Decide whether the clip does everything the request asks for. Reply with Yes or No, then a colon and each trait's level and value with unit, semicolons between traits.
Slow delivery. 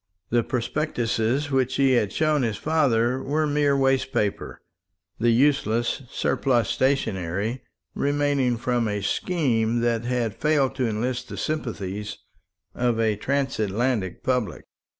Yes: slow, 125 wpm